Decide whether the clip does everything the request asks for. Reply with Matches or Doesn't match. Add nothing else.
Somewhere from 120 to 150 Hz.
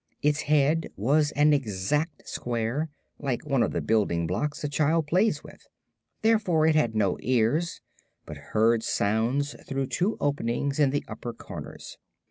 Matches